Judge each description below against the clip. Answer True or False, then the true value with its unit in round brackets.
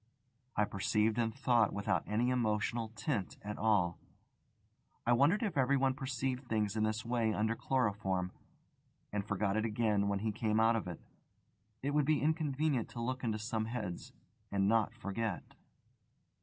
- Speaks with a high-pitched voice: False (110 Hz)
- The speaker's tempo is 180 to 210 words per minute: False (155 wpm)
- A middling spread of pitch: True (3.3 semitones)